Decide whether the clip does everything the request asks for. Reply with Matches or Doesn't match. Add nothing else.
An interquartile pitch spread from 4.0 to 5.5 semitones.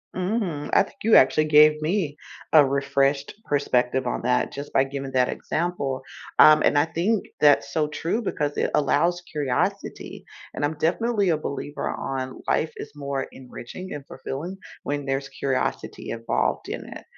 Doesn't match